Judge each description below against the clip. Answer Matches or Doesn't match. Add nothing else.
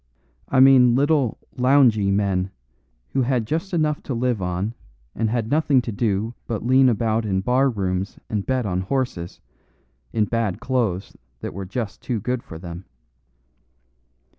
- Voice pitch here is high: Doesn't match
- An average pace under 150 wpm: Doesn't match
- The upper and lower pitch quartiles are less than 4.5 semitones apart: Doesn't match